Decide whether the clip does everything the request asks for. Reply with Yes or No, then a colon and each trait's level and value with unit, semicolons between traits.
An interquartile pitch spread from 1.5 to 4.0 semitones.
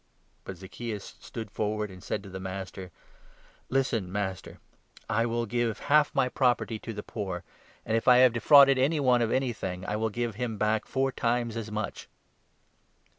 Yes: average, 3.3 semitones